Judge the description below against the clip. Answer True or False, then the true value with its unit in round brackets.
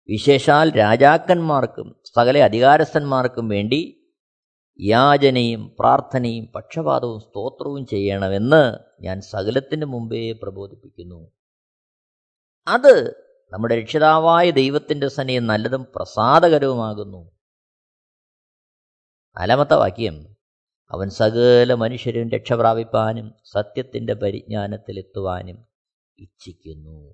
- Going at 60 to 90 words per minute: True (65 wpm)